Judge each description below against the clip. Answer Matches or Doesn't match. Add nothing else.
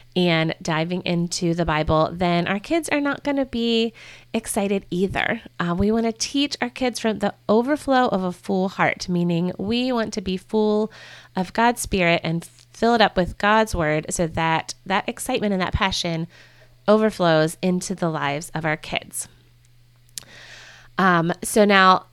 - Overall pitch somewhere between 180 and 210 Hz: Matches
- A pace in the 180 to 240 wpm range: Doesn't match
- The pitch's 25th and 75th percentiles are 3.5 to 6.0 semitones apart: Matches